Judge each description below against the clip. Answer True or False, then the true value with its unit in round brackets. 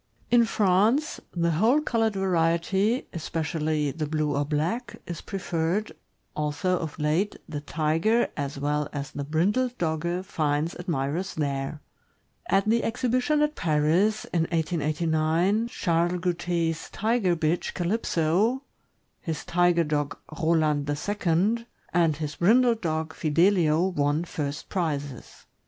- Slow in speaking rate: True (120 wpm)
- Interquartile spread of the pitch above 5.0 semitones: False (4.4 semitones)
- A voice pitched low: False (170 Hz)